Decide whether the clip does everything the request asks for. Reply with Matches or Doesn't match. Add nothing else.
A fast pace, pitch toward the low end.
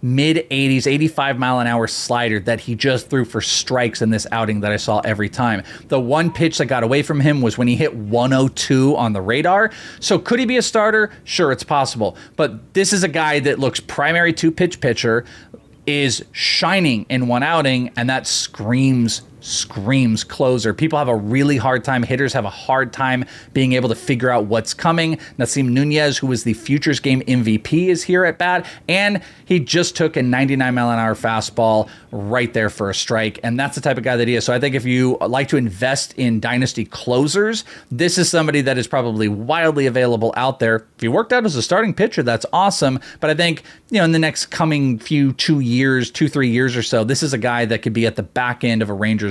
Matches